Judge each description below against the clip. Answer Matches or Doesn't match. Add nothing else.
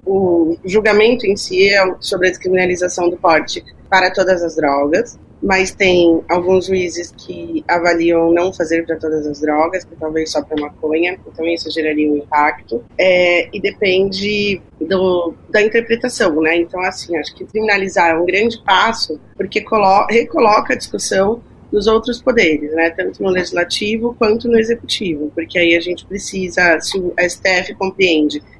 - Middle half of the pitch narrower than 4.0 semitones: Matches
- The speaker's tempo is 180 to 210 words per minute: Doesn't match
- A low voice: Doesn't match